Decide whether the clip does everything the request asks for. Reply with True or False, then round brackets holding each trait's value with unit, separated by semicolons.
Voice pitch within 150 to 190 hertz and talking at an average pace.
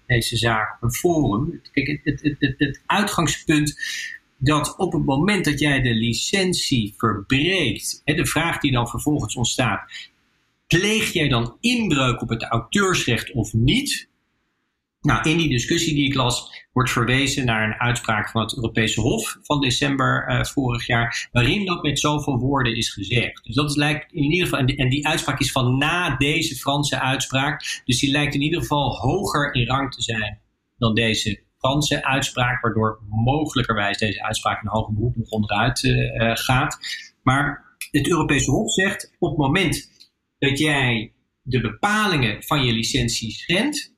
False (135 Hz; 170 wpm)